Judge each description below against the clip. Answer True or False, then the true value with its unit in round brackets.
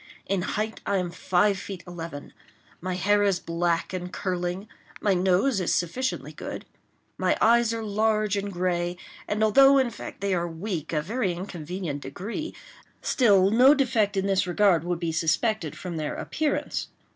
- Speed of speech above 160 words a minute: True (170 wpm)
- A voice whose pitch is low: False (190 Hz)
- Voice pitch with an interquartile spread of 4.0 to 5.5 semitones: False (3.5 semitones)